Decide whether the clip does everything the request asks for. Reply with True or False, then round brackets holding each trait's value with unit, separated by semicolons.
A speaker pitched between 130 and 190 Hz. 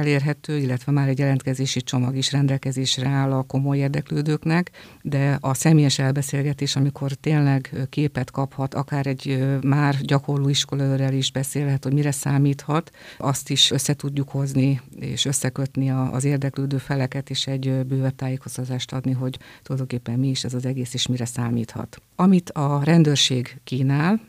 True (135 Hz)